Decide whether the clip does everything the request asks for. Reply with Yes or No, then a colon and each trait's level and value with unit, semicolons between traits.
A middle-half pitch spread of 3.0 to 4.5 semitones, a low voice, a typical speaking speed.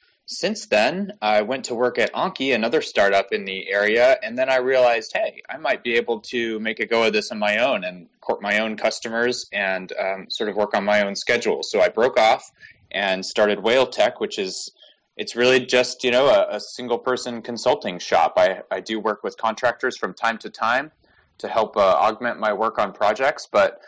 No: average, 3.3 semitones; low, 115 Hz; fast, 210 wpm